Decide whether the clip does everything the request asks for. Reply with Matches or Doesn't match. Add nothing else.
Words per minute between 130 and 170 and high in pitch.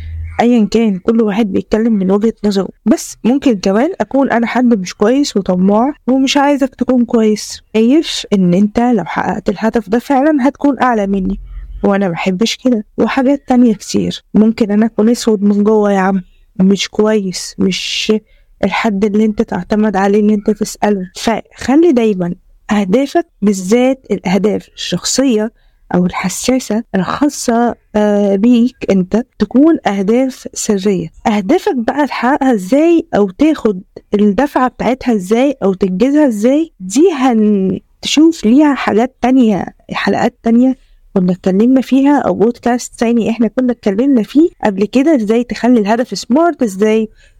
Matches